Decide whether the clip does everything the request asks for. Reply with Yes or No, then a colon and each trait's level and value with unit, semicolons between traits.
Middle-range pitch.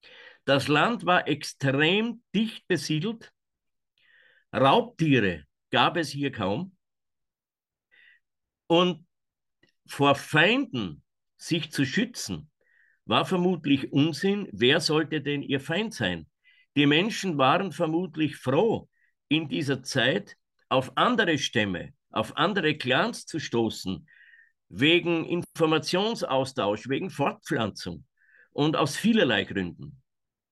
Yes: medium, 155 Hz